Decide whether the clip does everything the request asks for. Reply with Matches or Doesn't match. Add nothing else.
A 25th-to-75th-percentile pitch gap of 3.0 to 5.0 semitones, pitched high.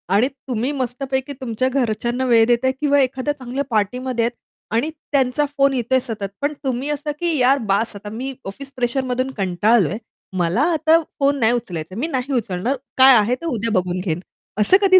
Matches